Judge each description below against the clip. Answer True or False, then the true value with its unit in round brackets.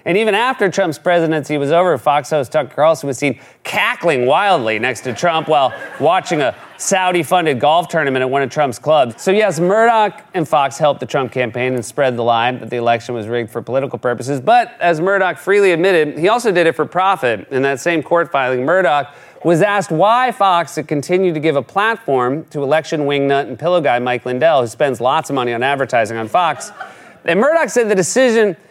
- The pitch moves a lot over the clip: True (5.7 semitones)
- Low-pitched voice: False (155 Hz)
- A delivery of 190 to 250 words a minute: True (205 wpm)